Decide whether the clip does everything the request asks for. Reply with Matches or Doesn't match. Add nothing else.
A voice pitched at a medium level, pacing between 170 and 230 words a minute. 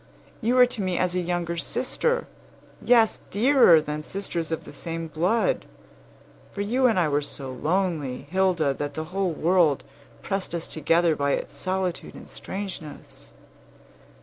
Doesn't match